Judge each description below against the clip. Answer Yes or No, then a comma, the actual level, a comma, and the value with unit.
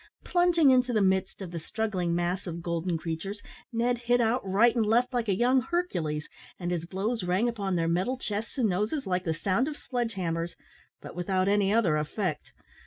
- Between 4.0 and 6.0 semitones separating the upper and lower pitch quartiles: Yes, average, 5.3 semitones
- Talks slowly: No, average, 195 wpm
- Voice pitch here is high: Yes, high, 200 Hz